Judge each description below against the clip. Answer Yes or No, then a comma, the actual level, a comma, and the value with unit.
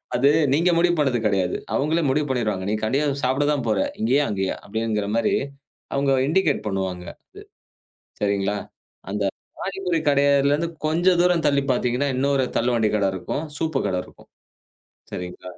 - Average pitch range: No, wide, 6.1 semitones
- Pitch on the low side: Yes, low, 130 Hz